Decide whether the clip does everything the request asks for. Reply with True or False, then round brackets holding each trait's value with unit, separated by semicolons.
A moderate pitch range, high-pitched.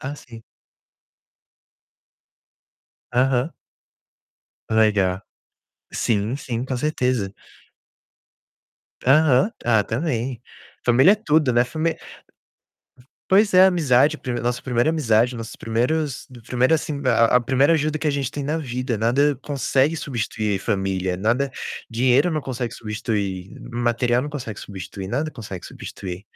False (4.4 semitones; 125 Hz)